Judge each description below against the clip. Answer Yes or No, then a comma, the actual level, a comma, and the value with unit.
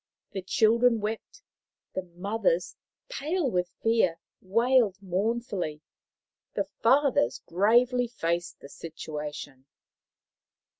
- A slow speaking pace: Yes, slow, 90 wpm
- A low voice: No, high, 200 Hz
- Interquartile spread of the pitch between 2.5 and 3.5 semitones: No, wide, 5.6 semitones